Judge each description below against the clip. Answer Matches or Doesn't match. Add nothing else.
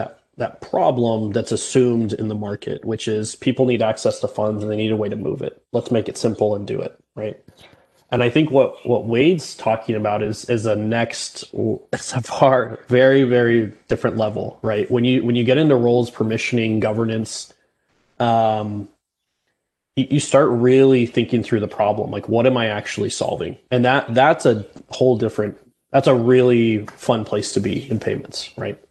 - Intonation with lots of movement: Doesn't match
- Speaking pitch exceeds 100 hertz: Matches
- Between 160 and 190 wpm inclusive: Matches